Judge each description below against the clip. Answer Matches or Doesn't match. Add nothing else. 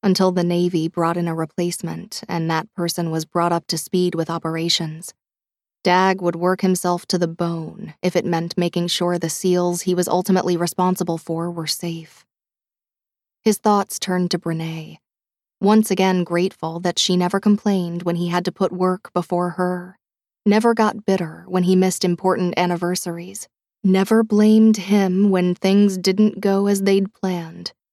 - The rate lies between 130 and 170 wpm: Matches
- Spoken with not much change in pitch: Matches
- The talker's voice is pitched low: Doesn't match